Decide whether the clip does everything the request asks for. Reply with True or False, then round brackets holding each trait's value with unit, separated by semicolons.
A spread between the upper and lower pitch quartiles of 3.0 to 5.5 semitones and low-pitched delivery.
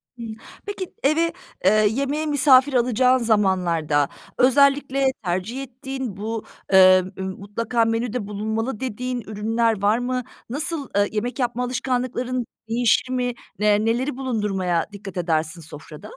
False (4.1 semitones; 235 Hz)